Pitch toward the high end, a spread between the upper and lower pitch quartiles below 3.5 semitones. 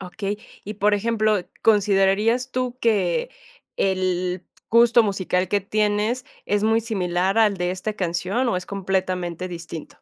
Yes: high, 200 Hz; average, 3.0 semitones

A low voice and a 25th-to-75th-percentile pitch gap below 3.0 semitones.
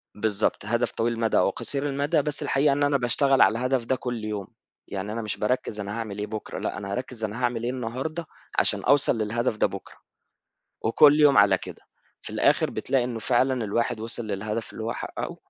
No: low, 115 Hz; average, 3.6 semitones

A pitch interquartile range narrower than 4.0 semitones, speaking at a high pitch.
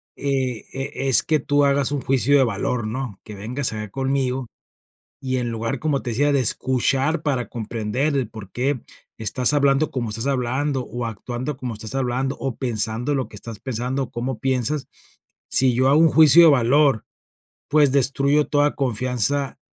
No: average, 2.9 semitones; low, 130 Hz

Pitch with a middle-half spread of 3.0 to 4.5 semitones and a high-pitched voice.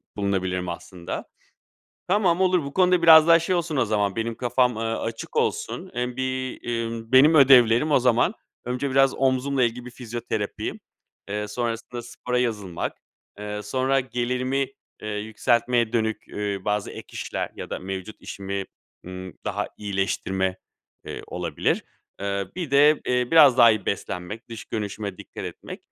No: average, 4.1 semitones; low, 120 Hz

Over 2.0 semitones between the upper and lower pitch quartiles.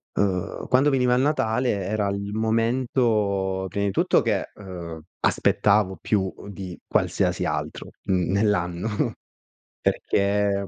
Yes: average, 2.7 semitones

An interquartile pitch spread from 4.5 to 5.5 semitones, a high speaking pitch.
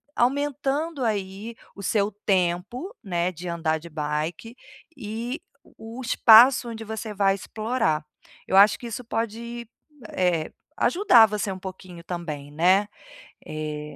Yes: average, 5.2 semitones; high, 205 Hz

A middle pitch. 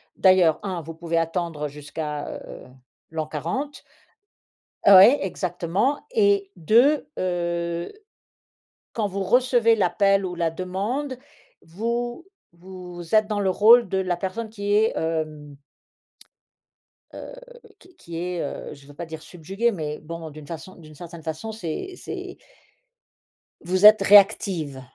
Yes: medium, 180 Hz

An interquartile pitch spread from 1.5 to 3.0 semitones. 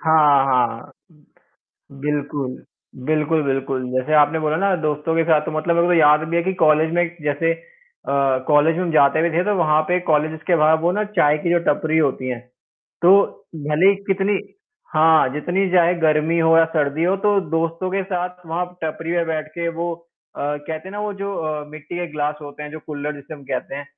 Yes: narrow, 2.6 semitones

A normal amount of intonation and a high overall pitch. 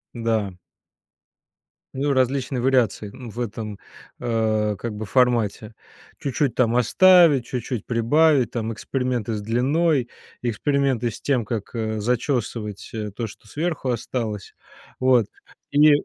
No: average, 3.4 semitones; low, 120 Hz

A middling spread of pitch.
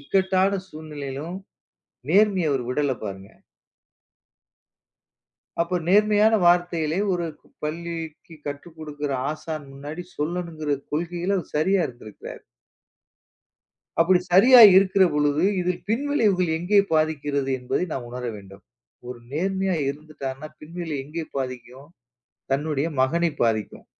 Yes: average, 4.1 semitones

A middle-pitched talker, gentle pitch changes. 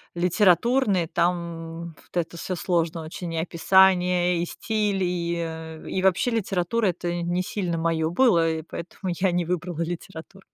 Yes: medium, 175 Hz; narrow, 2.0 semitones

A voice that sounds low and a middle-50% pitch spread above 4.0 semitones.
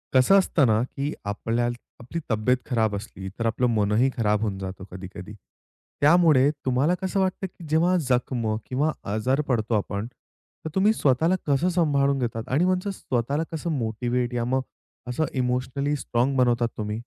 Yes: low, 125 Hz; average, 4.8 semitones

